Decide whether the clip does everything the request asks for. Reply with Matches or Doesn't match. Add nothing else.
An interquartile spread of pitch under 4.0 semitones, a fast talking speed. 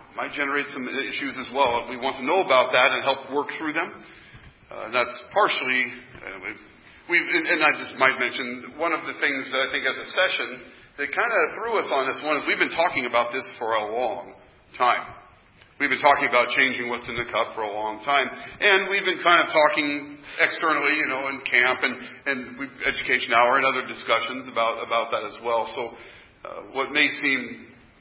Matches